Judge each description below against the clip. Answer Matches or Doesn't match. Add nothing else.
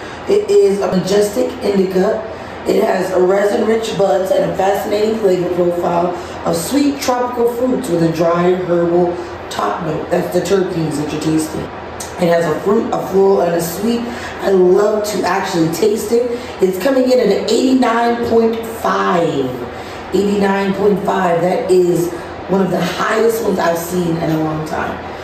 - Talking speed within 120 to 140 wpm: Doesn't match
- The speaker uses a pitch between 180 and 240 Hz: Matches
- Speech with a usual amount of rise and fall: Matches